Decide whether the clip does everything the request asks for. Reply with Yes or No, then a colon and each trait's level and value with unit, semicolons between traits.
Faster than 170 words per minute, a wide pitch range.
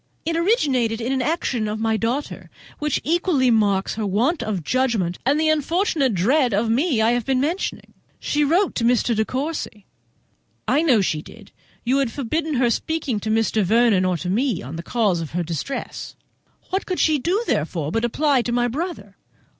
Yes: average, 185 wpm; wide, 5.7 semitones